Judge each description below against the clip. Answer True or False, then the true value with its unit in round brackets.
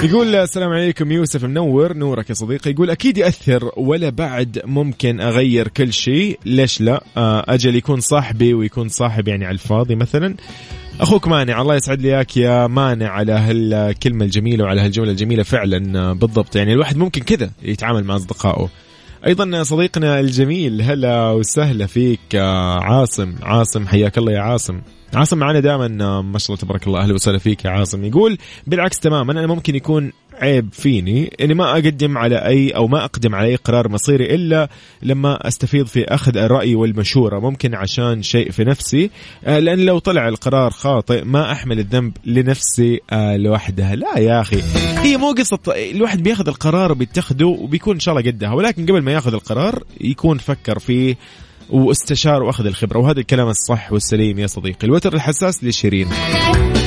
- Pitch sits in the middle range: False (125 Hz)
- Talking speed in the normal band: False (160 wpm)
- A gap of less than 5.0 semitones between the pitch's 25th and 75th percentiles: False (5.4 semitones)